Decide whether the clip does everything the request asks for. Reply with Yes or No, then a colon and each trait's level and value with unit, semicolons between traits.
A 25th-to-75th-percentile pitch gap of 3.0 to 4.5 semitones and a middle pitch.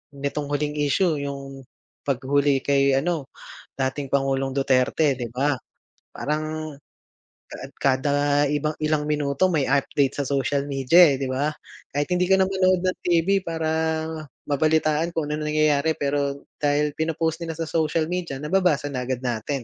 No: narrow, 2.4 semitones; medium, 145 Hz